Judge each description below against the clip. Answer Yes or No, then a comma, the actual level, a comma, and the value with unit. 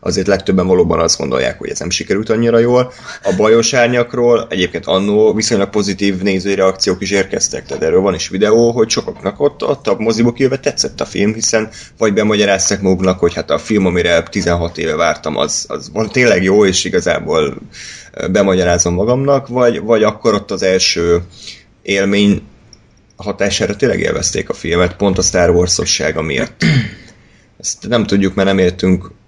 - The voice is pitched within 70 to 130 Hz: Yes, low, 100 Hz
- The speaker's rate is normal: No, fast, 165 wpm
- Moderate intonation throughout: Yes, average, 3.7 semitones